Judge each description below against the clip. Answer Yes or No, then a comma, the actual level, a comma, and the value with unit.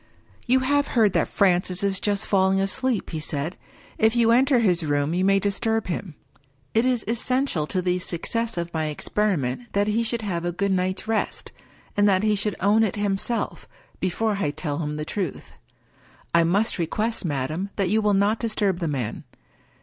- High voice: Yes, high, 195 Hz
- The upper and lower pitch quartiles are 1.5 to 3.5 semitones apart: No, average, 4.3 semitones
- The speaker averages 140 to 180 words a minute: No, average, 190 wpm